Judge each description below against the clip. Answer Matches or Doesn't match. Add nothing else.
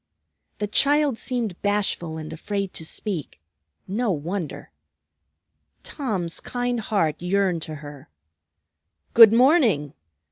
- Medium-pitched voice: Doesn't match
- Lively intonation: Matches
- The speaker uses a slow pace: Matches